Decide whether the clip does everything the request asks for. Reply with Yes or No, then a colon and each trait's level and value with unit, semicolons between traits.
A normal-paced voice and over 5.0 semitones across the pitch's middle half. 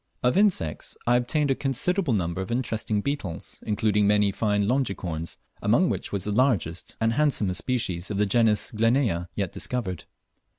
No: average, 160 wpm; average, 4.7 semitones